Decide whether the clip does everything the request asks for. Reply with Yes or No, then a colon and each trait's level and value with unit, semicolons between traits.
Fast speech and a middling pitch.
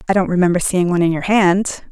Yes: fast, 250 wpm; medium, 180 Hz